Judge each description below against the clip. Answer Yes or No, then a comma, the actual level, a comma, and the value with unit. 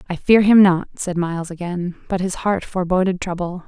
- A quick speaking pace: No, average, 195 wpm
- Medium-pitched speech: Yes, medium, 180 Hz